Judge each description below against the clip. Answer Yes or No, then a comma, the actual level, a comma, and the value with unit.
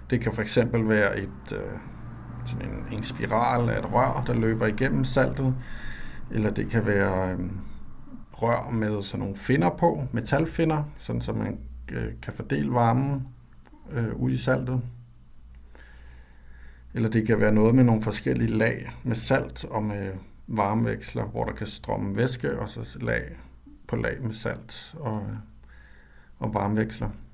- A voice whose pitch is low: Yes, low, 110 Hz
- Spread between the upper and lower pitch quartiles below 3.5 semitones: No, average, 3.8 semitones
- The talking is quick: No, slow, 145 wpm